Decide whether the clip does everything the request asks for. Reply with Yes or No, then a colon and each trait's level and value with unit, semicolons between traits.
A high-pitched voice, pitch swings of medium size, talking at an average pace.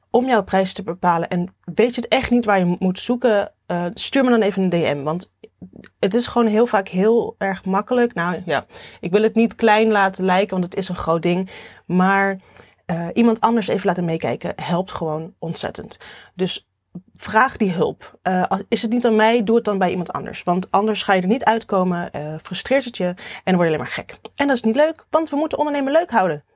No: high, 195 Hz; average, 4.3 semitones; fast, 225 wpm